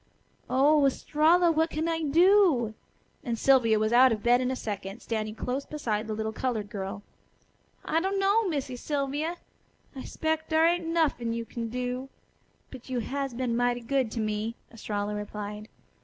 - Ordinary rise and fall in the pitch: No, wide, 5.7 semitones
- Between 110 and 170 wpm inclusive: Yes, average, 165 wpm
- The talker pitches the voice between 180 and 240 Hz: No, very high, 250 Hz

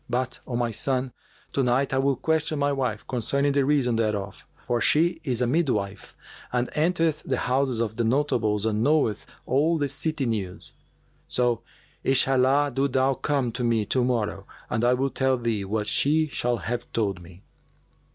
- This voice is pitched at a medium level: No, low, 125 Hz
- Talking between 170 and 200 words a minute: Yes, average, 175 wpm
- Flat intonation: No, average, 3.5 semitones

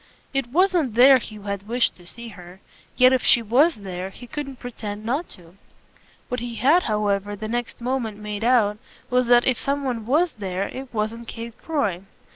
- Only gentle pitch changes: No, average, 3.8 semitones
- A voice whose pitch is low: No, high, 235 Hz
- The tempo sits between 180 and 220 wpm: Yes, average, 190 wpm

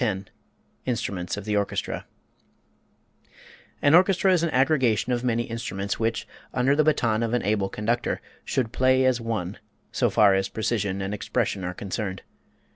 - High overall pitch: No, low, 115 Hz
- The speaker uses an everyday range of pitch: Yes, average, 4.1 semitones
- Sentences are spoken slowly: No, average, 155 wpm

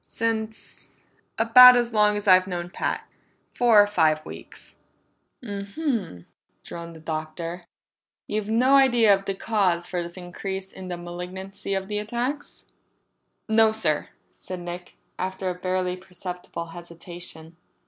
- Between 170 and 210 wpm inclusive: No, average, 140 wpm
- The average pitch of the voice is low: No, high, 190 Hz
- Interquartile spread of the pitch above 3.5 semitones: Yes, average, 3.9 semitones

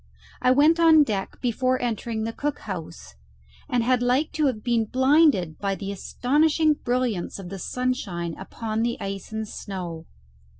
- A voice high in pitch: Yes, high, 235 Hz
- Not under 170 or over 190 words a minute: No, average, 160 wpm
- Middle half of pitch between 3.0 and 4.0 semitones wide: No, average, 4.8 semitones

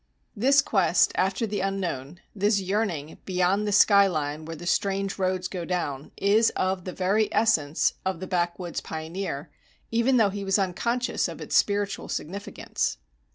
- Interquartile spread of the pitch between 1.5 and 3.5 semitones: Yes, average, 2.8 semitones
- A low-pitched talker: No, high, 190 Hz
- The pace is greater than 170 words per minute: No, average, 155 wpm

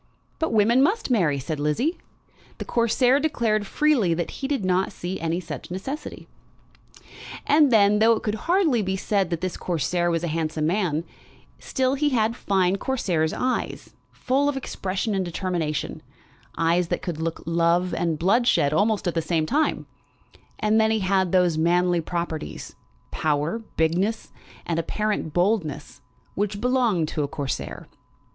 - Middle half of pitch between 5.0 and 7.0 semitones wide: Yes, wide, 5.5 semitones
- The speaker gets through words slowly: No, average, 155 wpm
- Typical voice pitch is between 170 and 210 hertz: Yes, high, 190 Hz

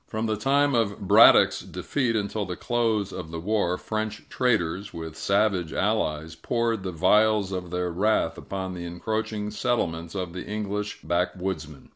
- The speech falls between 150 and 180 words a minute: Yes, average, 155 wpm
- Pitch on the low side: Yes, low, 100 Hz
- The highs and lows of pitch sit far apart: No, average, 3.8 semitones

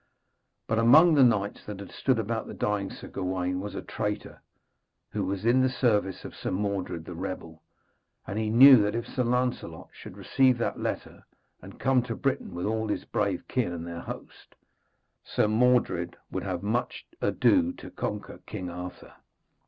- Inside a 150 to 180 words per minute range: Yes, average, 175 wpm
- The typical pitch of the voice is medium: No, low, 105 Hz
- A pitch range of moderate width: Yes, average, 4.9 semitones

